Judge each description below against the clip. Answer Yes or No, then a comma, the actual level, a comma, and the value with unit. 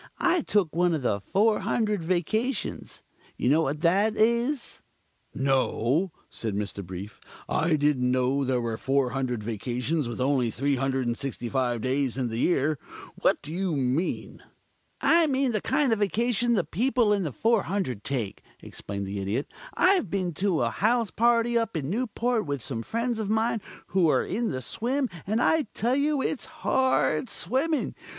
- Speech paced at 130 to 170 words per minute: Yes, average, 155 wpm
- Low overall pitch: No, medium, 170 Hz